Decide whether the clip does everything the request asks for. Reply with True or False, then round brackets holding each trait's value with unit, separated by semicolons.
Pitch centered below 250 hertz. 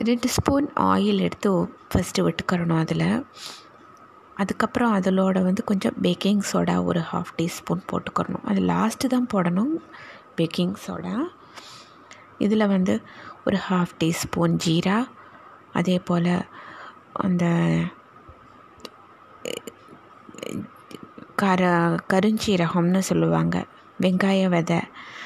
True (190 Hz)